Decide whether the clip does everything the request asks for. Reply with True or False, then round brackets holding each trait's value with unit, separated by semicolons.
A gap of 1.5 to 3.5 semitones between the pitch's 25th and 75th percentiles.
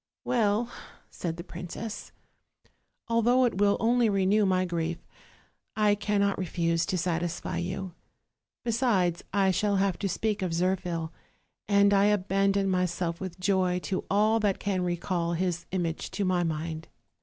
True (2.8 semitones)